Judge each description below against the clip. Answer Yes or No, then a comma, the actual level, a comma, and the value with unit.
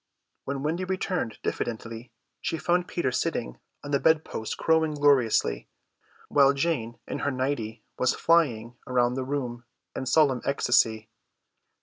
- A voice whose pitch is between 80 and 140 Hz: Yes, low, 135 Hz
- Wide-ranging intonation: No, average, 4.5 semitones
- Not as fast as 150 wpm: Yes, slow, 135 wpm